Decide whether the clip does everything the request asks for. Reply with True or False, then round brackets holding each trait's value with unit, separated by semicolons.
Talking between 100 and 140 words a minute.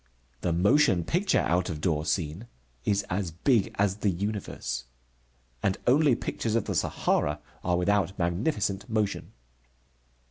True (135 wpm)